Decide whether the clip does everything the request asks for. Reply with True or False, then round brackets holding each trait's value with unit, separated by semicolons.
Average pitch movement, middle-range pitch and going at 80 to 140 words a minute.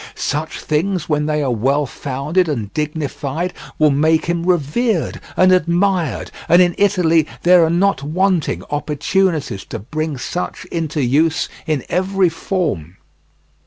True (3.6 semitones; 160 Hz; 135 wpm)